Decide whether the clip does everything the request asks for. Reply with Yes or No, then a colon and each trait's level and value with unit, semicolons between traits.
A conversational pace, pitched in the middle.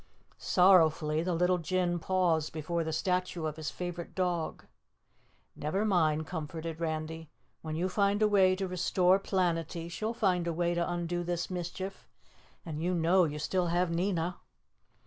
Yes: average, 155 wpm; medium, 175 Hz